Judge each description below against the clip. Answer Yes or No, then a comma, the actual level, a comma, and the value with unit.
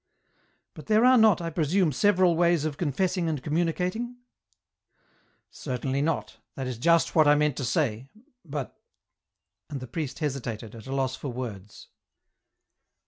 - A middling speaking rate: Yes, average, 160 wpm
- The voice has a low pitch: No, medium, 150 Hz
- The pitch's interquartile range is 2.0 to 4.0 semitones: No, average, 5.0 semitones